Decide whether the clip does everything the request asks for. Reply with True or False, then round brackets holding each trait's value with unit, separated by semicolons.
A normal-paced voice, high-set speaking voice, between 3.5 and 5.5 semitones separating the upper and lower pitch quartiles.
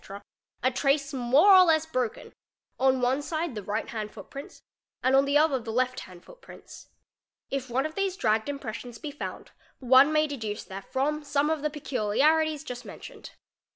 True (170 wpm; 275 Hz; 4.0 semitones)